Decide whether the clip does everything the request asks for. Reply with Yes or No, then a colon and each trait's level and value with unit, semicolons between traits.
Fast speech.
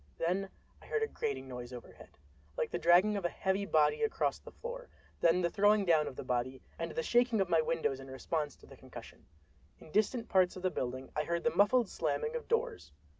Yes: fast, 220 wpm